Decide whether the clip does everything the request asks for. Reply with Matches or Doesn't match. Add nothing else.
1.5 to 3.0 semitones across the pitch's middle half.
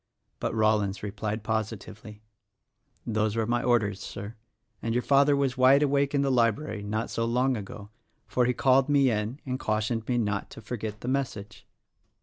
Doesn't match